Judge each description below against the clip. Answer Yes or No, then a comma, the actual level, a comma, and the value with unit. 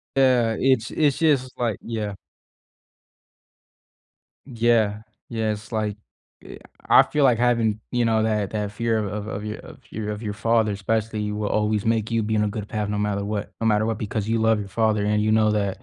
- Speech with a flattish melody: Yes, narrow, 1.5 semitones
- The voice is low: Yes, low, 110 Hz